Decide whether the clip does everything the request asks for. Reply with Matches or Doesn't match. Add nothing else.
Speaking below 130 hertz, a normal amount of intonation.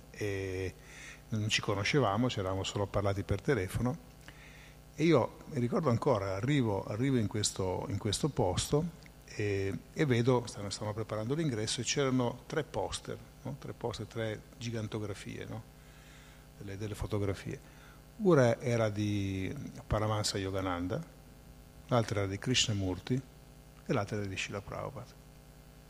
Matches